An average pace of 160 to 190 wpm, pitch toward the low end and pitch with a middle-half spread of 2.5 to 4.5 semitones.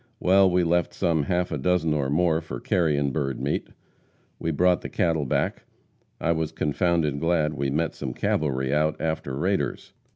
Yes: average, 170 wpm; very low, 80 Hz; average, 3.2 semitones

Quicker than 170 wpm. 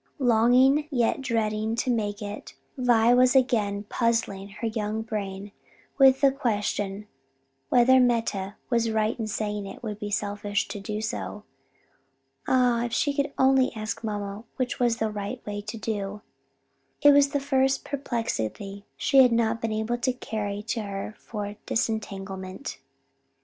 No: average, 150 wpm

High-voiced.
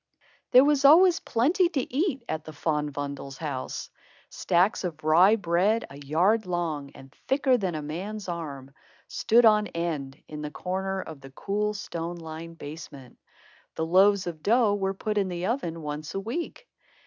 No: medium, 175 Hz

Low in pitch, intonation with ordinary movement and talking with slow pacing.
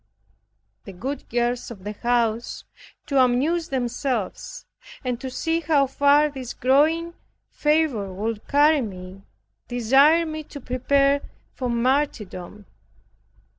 No: very high, 255 Hz; average, 3.9 semitones; slow, 115 wpm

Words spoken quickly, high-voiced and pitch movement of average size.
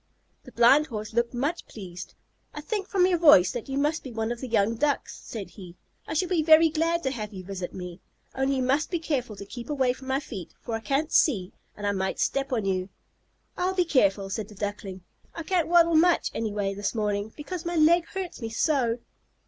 No: fast, 220 wpm; very high, 250 Hz; wide, 7.3 semitones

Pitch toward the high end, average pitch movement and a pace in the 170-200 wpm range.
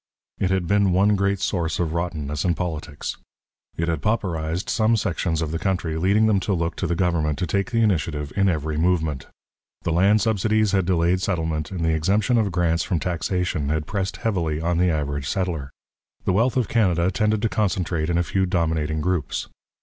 No: very low, 90 Hz; average, 3.5 semitones; average, 195 wpm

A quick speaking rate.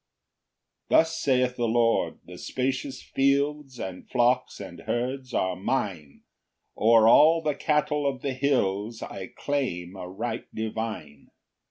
No: slow, 135 wpm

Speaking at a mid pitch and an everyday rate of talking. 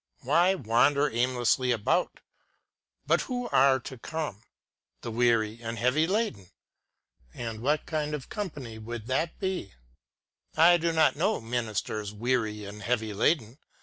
No: low, 125 Hz; average, 145 wpm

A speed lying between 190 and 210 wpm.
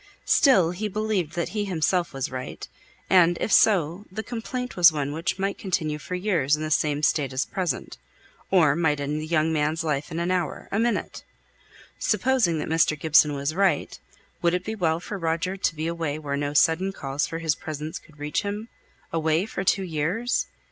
Yes: average, 195 wpm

